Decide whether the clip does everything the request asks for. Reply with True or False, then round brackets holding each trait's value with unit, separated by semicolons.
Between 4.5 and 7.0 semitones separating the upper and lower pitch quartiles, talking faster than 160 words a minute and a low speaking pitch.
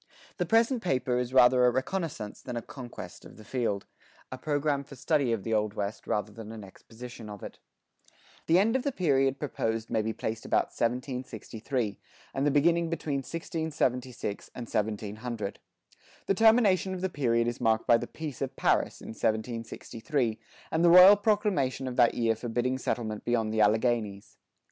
True (5.2 semitones; 170 wpm; 125 Hz)